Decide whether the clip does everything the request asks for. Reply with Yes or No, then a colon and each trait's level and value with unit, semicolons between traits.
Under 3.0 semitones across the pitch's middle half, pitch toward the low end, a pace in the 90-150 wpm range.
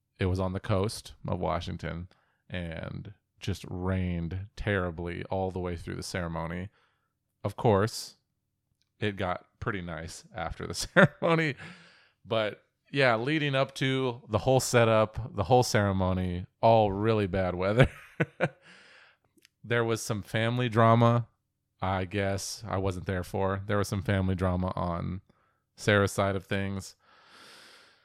No: average, 3.6 semitones; low, 100 Hz; slow, 135 wpm